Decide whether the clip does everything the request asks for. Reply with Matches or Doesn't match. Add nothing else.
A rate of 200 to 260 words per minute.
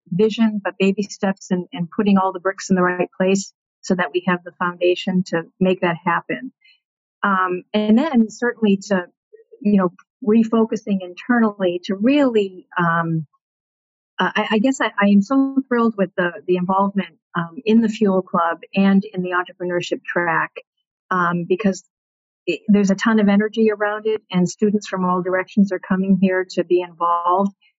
Doesn't match